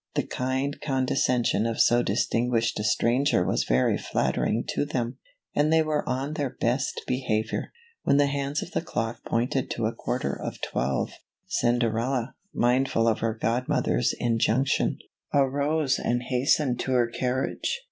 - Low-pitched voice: Yes, low, 125 Hz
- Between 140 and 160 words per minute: Yes, average, 150 wpm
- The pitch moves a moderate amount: Yes, average, 3.0 semitones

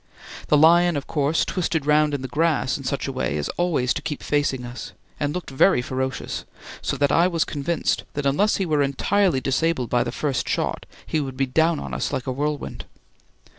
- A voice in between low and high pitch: Yes, medium, 145 Hz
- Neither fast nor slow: No, fast, 210 wpm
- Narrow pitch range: No, average, 3.6 semitones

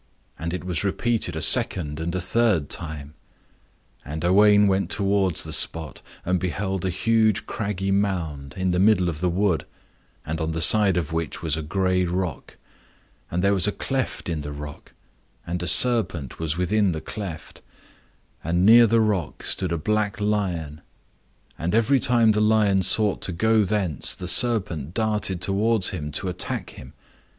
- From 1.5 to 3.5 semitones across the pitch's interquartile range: No, average, 4.2 semitones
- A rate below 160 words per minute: No, average, 170 wpm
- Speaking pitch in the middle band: No, very low, 95 Hz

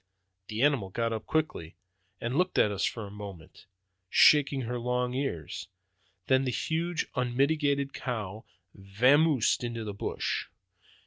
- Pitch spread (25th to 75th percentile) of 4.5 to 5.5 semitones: Yes, average, 4.9 semitones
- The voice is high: No, low, 125 Hz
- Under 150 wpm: Yes, slow, 135 wpm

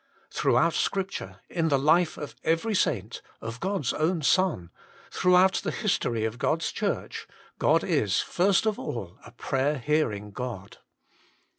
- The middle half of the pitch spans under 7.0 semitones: No, wide, 7.9 semitones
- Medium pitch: Yes, medium, 150 Hz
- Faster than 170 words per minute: No, average, 150 wpm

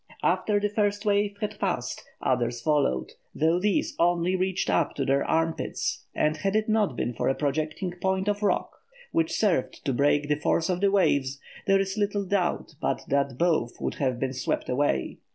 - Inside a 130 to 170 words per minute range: No, average, 190 wpm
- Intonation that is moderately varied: No, wide, 6.2 semitones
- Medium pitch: Yes, medium, 175 Hz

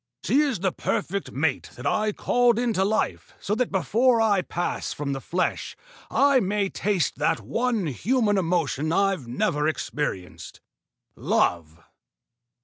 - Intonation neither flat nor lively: No, wide, 7.1 semitones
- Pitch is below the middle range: No, high, 190 Hz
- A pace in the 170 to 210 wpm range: No, average, 140 wpm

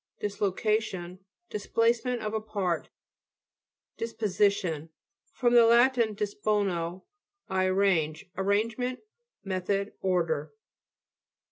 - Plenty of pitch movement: No, average, 3.2 semitones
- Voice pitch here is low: No, high, 200 Hz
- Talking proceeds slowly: Yes, slow, 75 wpm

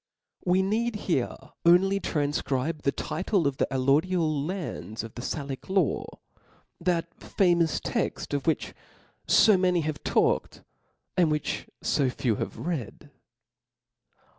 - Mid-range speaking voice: Yes, medium, 160 Hz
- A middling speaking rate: No, slow, 120 wpm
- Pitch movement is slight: No, average, 4.7 semitones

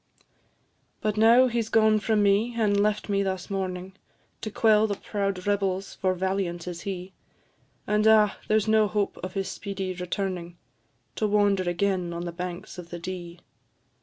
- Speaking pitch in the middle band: No, high, 195 Hz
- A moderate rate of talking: Yes, average, 165 wpm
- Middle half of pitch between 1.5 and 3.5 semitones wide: Yes, narrow, 2.6 semitones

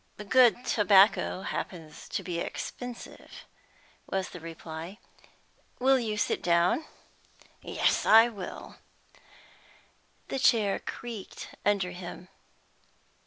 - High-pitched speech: Yes, high, 200 Hz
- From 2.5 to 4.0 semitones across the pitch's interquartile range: No, average, 4.7 semitones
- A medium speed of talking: No, slow, 95 wpm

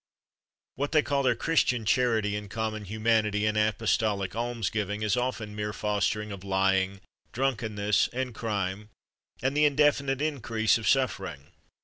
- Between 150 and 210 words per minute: No, average, 140 wpm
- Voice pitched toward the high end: No, low, 110 Hz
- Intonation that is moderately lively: Yes, average, 3.3 semitones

